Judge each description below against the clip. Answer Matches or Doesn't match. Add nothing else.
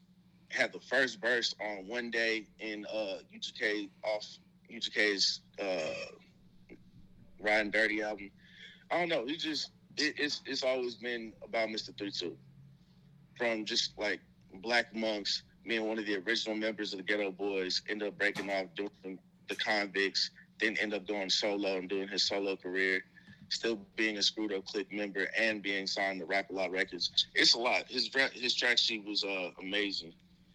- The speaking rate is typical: Matches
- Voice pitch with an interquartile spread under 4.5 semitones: Matches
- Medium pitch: Doesn't match